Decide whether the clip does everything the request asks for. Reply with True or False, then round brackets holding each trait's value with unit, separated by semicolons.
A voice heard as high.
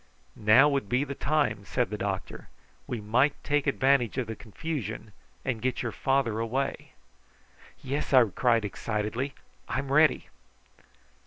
False (130 Hz)